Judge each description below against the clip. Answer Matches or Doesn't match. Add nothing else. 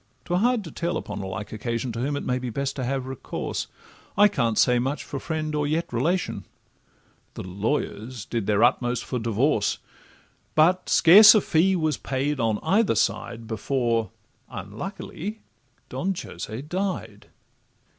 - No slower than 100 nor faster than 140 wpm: Doesn't match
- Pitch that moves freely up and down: Matches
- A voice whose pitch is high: Doesn't match